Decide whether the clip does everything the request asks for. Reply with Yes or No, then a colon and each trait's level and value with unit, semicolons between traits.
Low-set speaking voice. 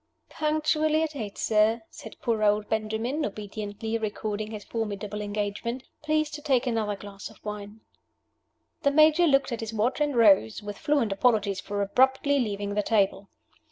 No: high, 220 Hz